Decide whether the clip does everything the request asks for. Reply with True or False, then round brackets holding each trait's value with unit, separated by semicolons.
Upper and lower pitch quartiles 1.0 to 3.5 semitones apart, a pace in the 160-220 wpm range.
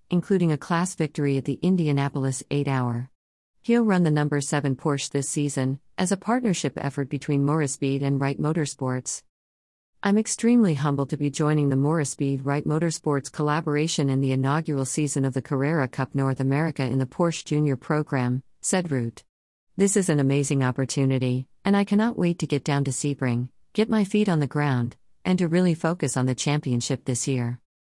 True (3.2 semitones; 180 wpm)